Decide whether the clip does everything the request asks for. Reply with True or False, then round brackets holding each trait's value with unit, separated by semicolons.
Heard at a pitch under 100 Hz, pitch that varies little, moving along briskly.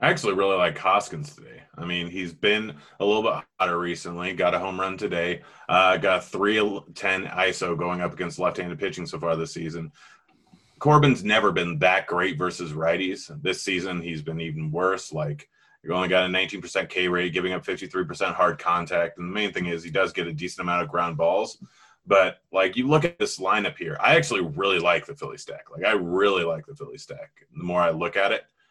True (90 Hz; 2.0 semitones; 215 wpm)